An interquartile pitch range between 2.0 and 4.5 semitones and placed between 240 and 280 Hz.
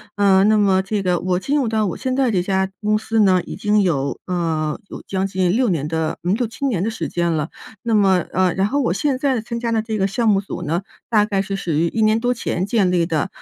No: average, 3.7 semitones; high, 195 Hz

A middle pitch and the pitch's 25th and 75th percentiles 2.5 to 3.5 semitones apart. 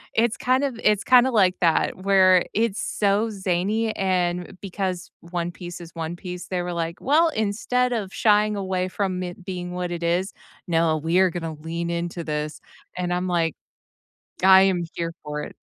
Yes: medium, 180 Hz; average, 2.8 semitones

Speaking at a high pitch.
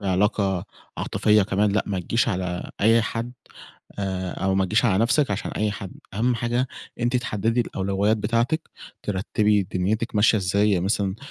No: low, 105 Hz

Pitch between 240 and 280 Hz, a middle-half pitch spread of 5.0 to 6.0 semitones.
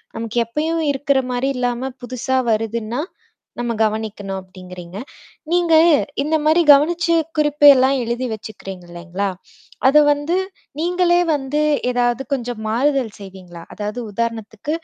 Yes: high, 245 Hz; average, 5.3 semitones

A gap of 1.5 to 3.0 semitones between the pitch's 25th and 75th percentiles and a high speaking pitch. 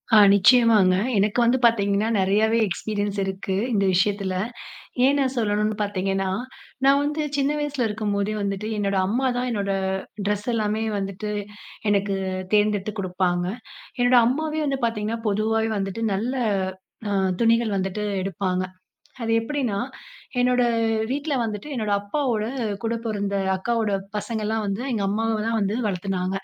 Yes: average, 2.7 semitones; high, 210 Hz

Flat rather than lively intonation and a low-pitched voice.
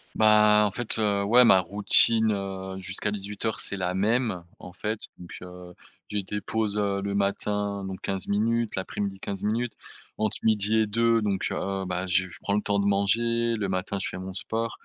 Yes: narrow, 2.2 semitones; low, 100 Hz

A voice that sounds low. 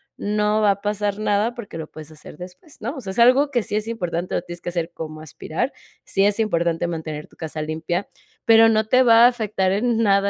No: high, 205 Hz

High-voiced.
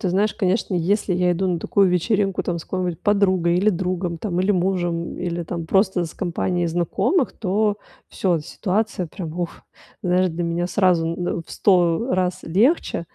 No: medium, 180 Hz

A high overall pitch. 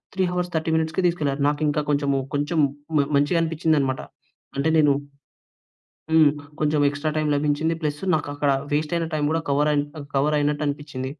No: medium, 150 Hz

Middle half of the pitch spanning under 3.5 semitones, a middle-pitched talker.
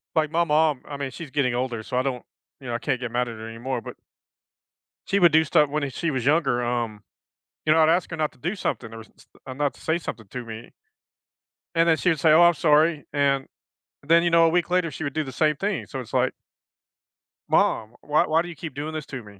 No: average, 4.4 semitones; medium, 145 Hz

